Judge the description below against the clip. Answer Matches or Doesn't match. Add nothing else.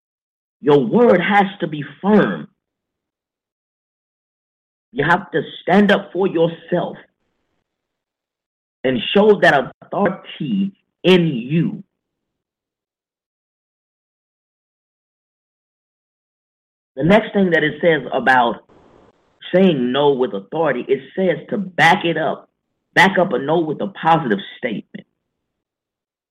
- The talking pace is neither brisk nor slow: Doesn't match